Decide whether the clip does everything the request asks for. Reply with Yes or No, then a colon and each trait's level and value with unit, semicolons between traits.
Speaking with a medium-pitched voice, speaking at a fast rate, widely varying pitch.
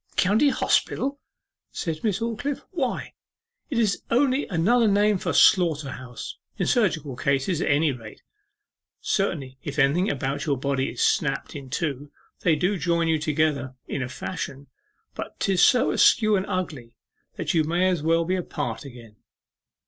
No: medium, 160 Hz; average, 155 wpm; wide, 5.9 semitones